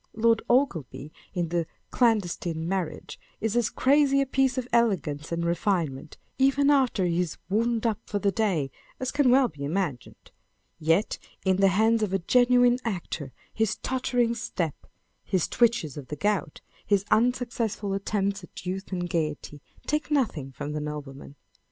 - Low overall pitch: No, high, 200 Hz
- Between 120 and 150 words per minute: No, average, 165 wpm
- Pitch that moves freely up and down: Yes, wide, 6.2 semitones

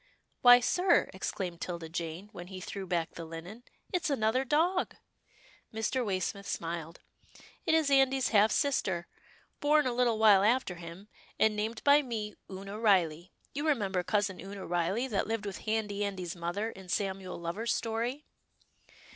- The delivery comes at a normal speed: Yes, average, 160 wpm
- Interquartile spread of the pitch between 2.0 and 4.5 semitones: No, average, 5.1 semitones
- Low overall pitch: No, high, 205 Hz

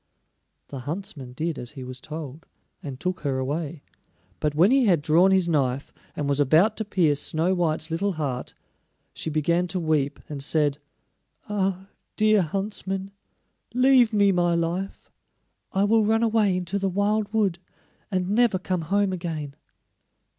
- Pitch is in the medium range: Yes, medium, 175 Hz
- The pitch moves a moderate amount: Yes, average, 4.8 semitones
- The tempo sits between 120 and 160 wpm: Yes, average, 155 wpm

